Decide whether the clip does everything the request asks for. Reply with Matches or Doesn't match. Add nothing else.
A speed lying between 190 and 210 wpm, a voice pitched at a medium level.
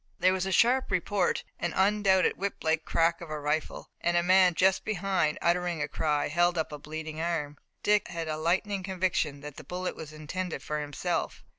Matches